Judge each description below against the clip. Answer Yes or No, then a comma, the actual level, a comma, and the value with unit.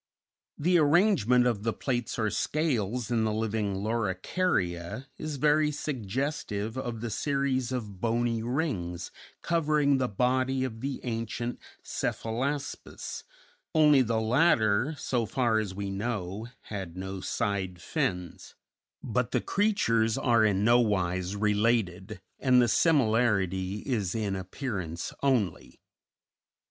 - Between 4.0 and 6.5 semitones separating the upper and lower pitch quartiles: Yes, average, 4.5 semitones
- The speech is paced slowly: Yes, slow, 120 wpm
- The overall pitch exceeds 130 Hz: No, low, 115 Hz